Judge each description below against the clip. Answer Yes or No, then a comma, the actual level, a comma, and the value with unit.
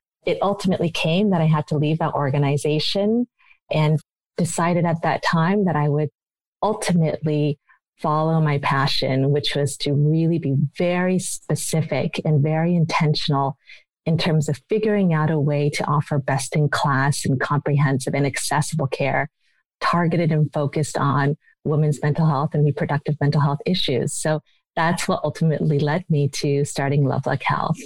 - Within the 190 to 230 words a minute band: No, average, 155 wpm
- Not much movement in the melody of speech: Yes, narrow, 2.2 semitones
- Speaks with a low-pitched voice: No, medium, 150 Hz